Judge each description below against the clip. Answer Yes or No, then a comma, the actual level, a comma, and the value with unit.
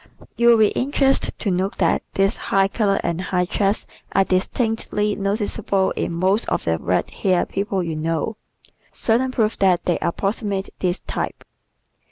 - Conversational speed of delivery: Yes, average, 160 wpm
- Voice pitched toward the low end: No, high, 195 Hz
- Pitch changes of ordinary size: Yes, average, 3.0 semitones